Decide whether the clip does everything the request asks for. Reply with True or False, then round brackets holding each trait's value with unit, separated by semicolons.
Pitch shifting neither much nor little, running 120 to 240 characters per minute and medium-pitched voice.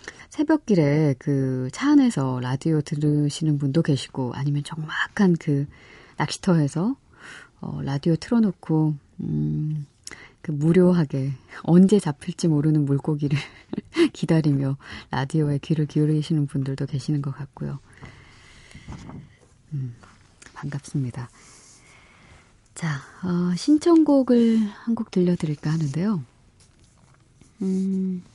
True (4.7 semitones; 230 characters per minute; 150 Hz)